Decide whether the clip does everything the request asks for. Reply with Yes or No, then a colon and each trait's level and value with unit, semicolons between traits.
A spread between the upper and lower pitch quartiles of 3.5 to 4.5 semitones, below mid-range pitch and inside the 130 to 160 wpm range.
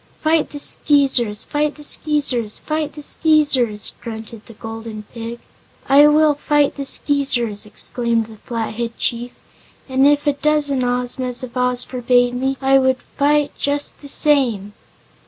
No: average, 3.8 semitones; very high, 260 Hz; average, 145 wpm